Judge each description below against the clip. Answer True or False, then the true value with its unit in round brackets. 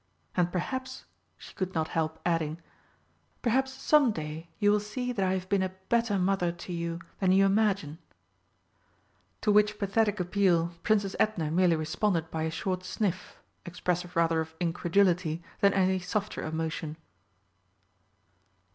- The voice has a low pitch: False (185 Hz)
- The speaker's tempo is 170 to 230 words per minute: False (145 wpm)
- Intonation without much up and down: False (3.7 semitones)